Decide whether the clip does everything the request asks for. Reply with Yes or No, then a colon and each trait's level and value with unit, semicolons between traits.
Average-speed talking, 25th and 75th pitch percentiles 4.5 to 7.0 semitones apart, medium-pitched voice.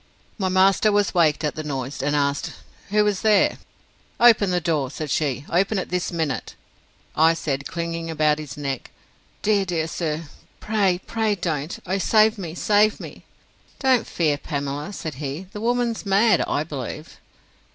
Yes: average, 160 wpm; wide, 5.4 semitones; medium, 170 Hz